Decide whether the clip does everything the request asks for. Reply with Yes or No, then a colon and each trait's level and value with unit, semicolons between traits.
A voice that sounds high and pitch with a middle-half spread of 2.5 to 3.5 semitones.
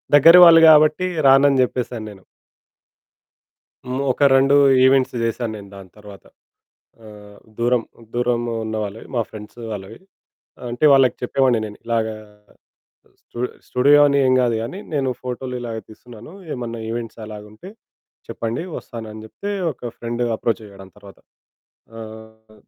No: low, 115 Hz; average, 3.2 semitones